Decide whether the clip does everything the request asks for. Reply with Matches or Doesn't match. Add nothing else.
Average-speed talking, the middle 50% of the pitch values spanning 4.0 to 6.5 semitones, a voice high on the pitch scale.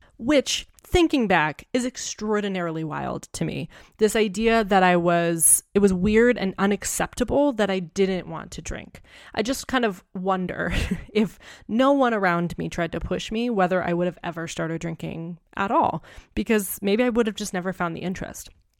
Matches